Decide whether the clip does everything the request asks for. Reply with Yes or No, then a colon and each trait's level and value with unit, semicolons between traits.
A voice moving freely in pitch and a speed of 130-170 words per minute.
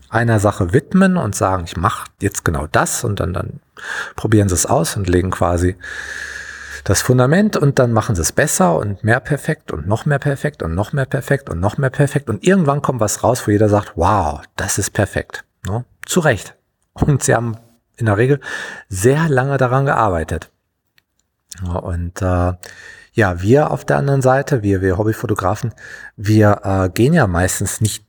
No: wide, 6.1 semitones; average, 185 wpm